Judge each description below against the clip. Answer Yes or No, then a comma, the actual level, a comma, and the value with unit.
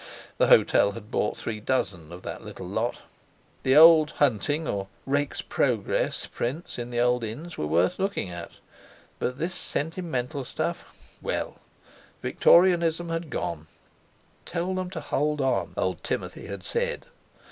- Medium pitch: Yes, medium, 145 Hz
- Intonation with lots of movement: Yes, wide, 7.0 semitones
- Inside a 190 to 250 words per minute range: No, slow, 135 wpm